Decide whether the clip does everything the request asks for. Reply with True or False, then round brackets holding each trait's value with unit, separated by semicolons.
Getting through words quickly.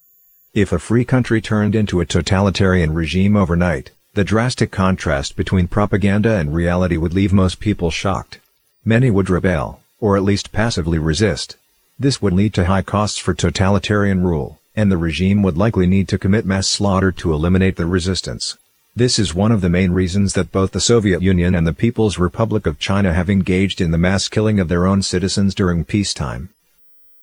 False (185 wpm)